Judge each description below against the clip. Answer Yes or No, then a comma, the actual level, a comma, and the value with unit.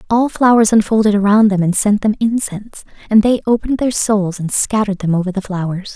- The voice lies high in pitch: Yes, high, 210 Hz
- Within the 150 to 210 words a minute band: Yes, average, 200 wpm